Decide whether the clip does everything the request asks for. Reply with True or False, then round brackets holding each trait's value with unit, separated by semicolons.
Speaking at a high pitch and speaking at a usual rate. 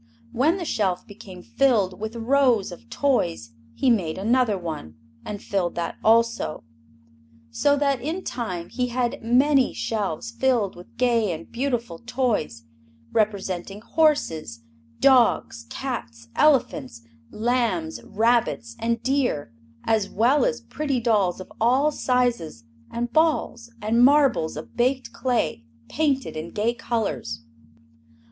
False (230 Hz; 125 wpm)